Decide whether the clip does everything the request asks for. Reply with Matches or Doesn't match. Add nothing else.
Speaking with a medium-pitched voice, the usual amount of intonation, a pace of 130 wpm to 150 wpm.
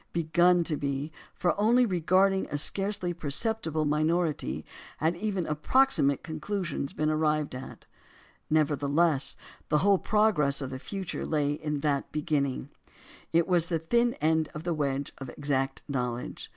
Matches